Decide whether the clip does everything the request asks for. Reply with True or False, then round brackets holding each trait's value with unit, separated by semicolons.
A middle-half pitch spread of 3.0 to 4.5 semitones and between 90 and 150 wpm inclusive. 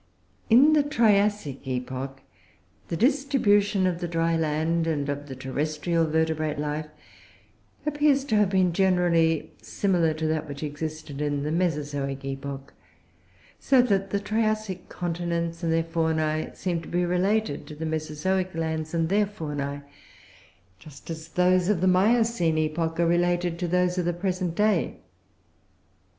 True (3.5 semitones; 145 wpm)